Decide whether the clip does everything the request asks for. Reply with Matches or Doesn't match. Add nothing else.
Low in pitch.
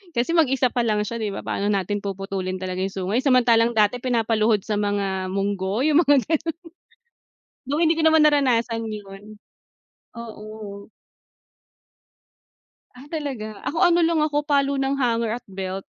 Doesn't match